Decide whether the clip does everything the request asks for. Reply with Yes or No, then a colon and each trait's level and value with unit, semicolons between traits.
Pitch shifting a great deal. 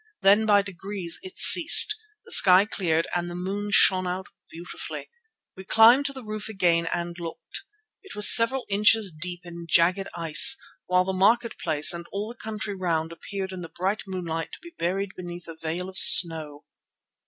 No: average, 3.5 semitones